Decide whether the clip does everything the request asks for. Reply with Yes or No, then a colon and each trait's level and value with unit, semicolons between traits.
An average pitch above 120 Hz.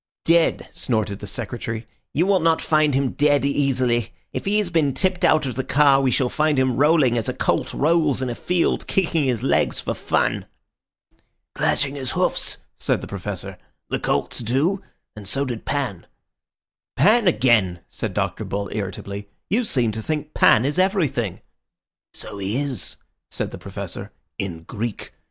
Yes: low, 135 Hz